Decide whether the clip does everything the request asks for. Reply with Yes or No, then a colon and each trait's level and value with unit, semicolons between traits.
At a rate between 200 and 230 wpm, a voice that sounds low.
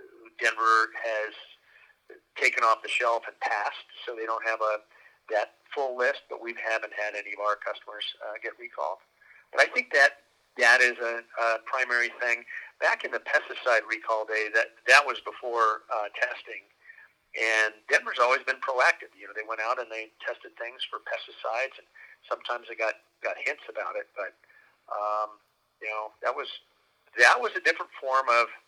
No: average, 180 wpm; low, 110 Hz